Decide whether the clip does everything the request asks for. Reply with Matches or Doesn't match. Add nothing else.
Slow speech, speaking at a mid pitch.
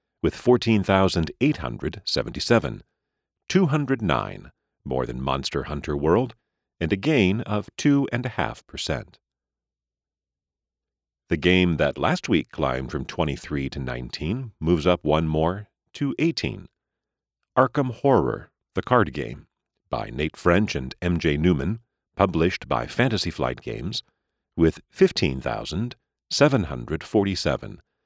Doesn't match